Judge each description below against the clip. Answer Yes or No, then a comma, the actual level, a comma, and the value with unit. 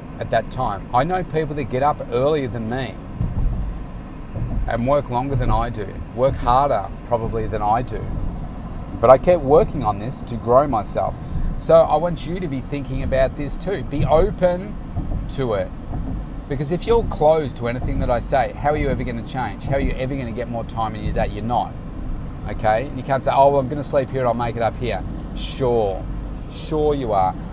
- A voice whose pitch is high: No, low, 130 Hz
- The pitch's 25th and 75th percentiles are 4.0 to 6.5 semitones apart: Yes, average, 4.3 semitones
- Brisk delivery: Yes, fast, 215 wpm